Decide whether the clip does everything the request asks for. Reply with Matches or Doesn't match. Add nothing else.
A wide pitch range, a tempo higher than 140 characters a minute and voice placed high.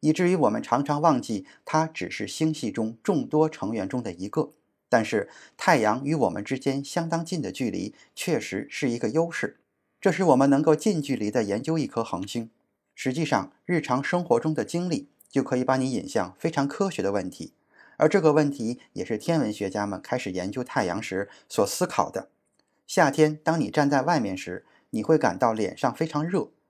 Doesn't match